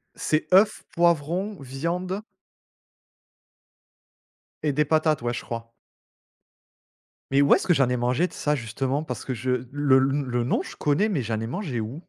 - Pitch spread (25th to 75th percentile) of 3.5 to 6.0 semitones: Yes, average, 4.6 semitones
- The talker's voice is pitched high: No, medium, 140 Hz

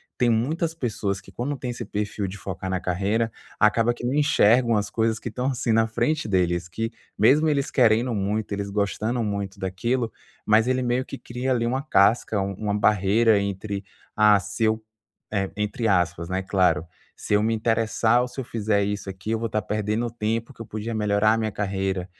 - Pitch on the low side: Yes, low, 110 Hz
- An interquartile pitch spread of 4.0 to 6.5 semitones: No, average, 2.9 semitones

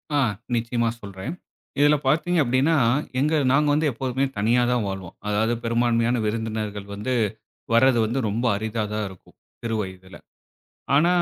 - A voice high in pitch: No, low, 115 Hz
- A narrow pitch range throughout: No, average, 3.7 semitones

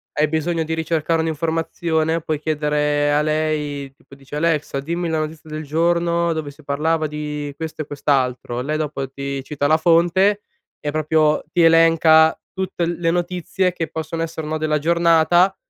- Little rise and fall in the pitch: Yes, narrow, 1.9 semitones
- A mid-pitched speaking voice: Yes, medium, 155 Hz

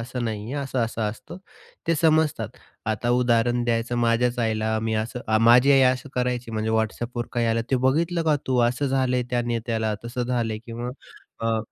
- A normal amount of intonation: No, narrow, 2.0 semitones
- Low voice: Yes, low, 120 Hz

